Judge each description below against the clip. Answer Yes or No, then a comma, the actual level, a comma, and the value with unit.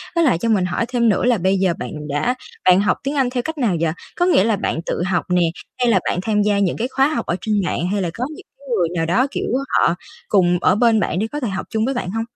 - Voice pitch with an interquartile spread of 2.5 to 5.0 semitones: No, wide, 5.4 semitones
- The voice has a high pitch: Yes, high, 210 Hz